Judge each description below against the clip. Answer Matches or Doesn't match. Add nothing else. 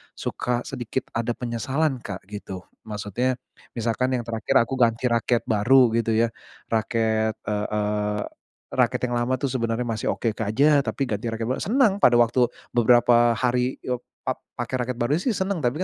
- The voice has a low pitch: Matches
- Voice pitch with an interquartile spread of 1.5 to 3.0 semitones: Matches